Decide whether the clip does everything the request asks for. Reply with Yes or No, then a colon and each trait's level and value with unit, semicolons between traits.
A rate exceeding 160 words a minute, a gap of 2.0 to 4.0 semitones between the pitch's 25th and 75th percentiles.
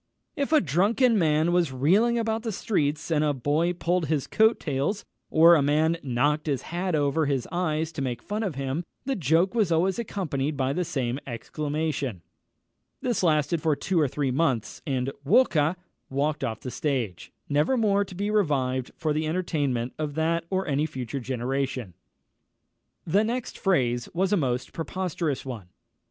No: average, 170 wpm; average, 5.0 semitones